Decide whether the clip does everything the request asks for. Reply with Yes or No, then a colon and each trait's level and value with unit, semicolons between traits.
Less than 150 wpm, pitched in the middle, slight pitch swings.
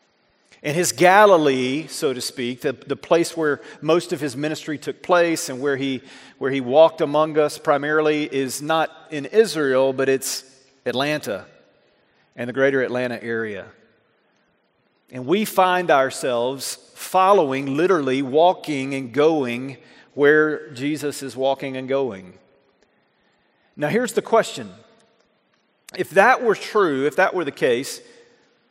No: slow, 135 wpm; medium, 145 Hz; average, 3.1 semitones